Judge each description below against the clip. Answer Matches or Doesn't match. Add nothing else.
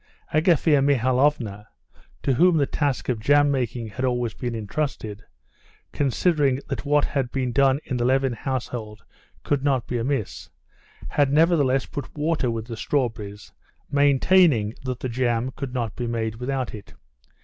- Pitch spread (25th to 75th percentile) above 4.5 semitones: Doesn't match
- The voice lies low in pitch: Matches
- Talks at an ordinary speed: Matches